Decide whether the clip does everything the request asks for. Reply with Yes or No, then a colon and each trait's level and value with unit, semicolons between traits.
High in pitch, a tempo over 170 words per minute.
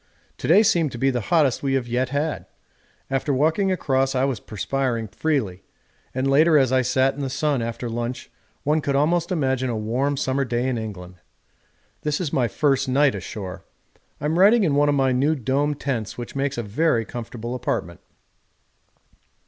No: low, 135 Hz; average, 180 wpm